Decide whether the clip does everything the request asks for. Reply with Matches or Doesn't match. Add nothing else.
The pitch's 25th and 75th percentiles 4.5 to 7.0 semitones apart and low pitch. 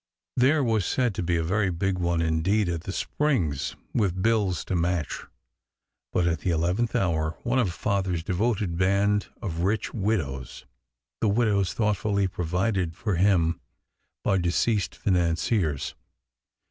Doesn't match